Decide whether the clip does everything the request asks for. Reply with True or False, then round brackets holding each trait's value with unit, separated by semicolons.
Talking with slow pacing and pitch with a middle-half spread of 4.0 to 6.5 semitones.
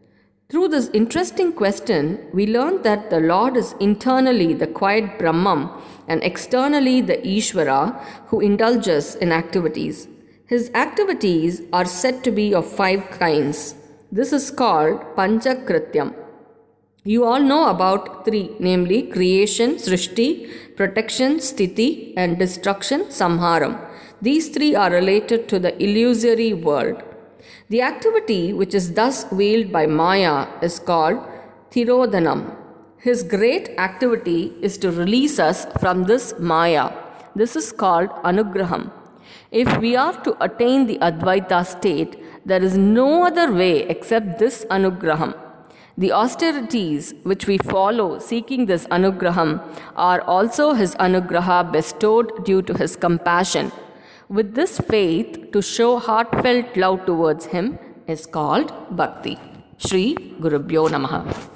True (125 wpm; 5.1 semitones)